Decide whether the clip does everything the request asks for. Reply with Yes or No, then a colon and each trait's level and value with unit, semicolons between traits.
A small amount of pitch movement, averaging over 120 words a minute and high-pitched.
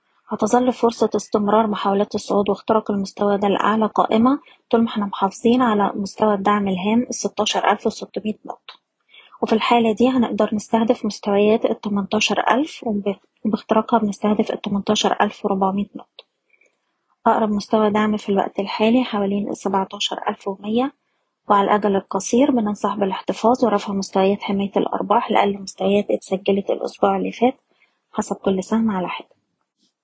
Yes: narrow, 2.2 semitones; average, 130 wpm; high, 210 Hz